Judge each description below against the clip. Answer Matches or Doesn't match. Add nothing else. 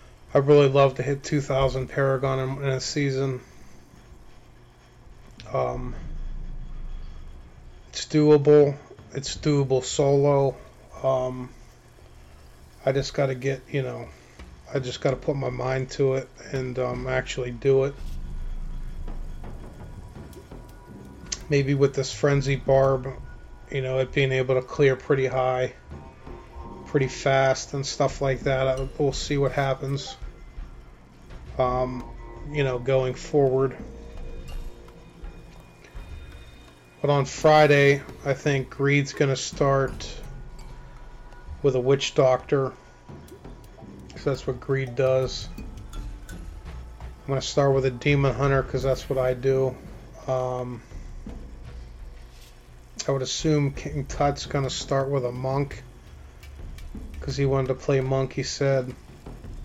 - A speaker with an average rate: Doesn't match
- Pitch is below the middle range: Matches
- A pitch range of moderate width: Doesn't match